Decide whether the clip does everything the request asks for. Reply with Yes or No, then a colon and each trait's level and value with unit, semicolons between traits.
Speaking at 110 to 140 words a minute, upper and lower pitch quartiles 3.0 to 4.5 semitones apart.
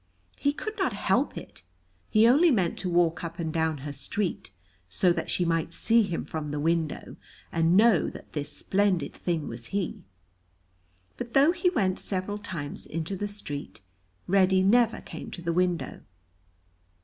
No: average, 165 wpm; average, 4.1 semitones